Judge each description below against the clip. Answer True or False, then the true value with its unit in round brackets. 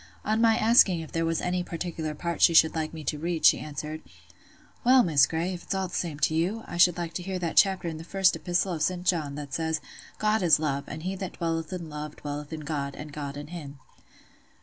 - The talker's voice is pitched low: False (165 Hz)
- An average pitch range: True (3.0 semitones)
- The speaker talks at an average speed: False (240 wpm)